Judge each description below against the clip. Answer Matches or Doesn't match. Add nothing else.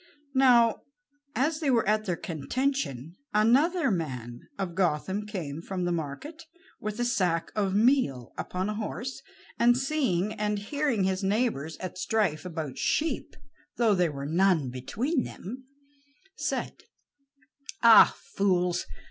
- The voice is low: Doesn't match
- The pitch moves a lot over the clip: Matches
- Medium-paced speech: Doesn't match